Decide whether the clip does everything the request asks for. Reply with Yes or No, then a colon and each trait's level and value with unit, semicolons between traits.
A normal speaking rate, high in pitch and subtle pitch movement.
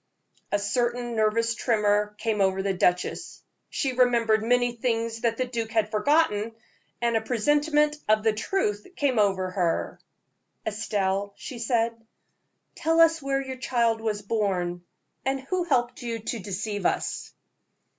No: average, 145 wpm; high, 225 Hz; average, 3.1 semitones